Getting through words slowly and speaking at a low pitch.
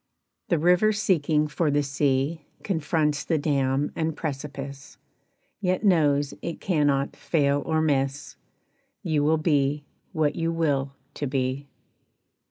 No: slow, 125 wpm; medium, 150 Hz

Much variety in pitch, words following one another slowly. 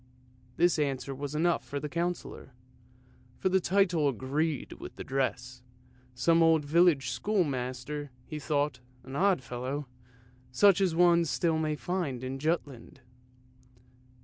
No: average, 4.4 semitones; slow, 130 wpm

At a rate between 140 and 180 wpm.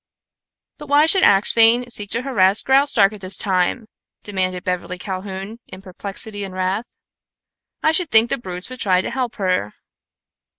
Yes: average, 160 wpm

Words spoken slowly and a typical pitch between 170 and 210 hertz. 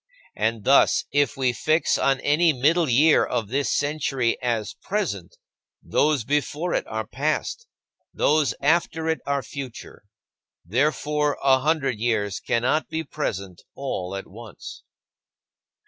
No: slow, 130 wpm; medium, 140 Hz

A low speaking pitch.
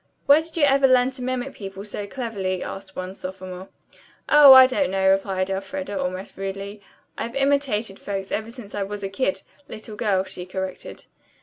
No: high, 200 Hz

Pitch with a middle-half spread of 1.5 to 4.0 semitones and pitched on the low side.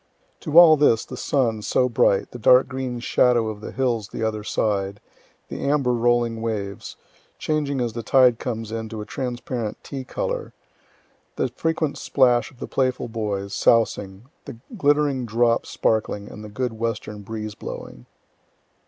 Yes: average, 3.2 semitones; low, 115 Hz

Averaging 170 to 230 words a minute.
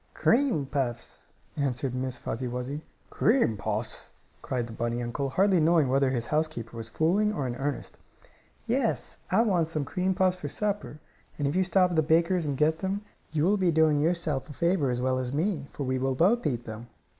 Yes: average, 200 wpm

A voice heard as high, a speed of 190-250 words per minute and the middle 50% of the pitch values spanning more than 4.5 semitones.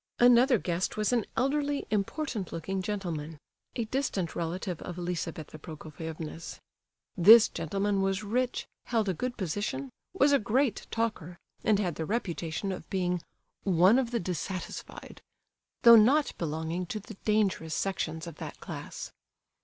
No: high, 195 Hz; average, 140 wpm; average, 5.3 semitones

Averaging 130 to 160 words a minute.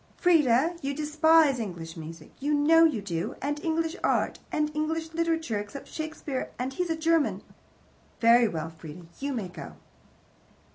Yes: average, 150 wpm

